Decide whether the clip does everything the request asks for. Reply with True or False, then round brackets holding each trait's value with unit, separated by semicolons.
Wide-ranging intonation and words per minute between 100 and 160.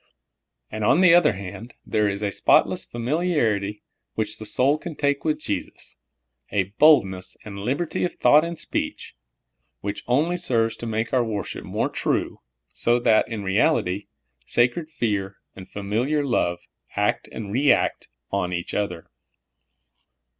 True (6.3 semitones; 155 wpm)